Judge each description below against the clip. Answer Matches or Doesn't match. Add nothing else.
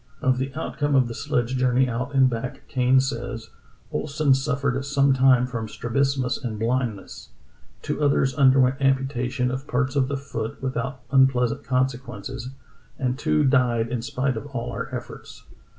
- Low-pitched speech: Matches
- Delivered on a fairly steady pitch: Matches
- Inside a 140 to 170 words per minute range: Matches